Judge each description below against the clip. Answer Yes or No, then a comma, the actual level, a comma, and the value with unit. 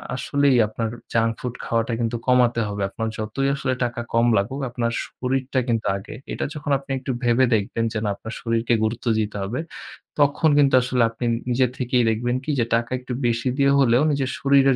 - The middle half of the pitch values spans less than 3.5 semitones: Yes, narrow, 2.6 semitones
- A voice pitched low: Yes, low, 120 Hz